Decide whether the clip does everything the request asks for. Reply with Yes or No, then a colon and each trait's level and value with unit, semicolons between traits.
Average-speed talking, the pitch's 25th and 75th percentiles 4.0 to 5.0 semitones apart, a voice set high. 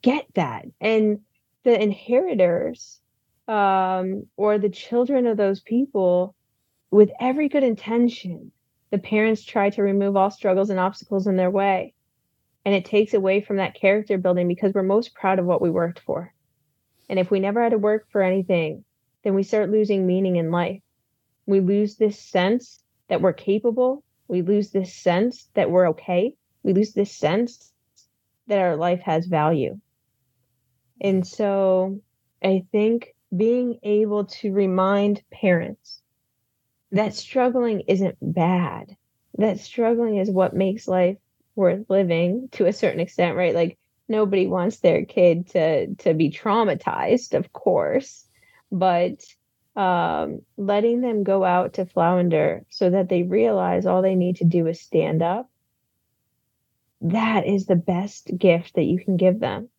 No: average, 150 wpm; average, 3.0 semitones; high, 195 Hz